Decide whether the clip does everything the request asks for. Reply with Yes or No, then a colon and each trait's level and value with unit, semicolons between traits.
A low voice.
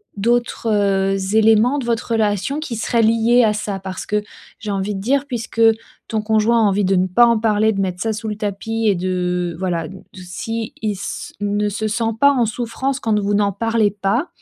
No: high, 215 Hz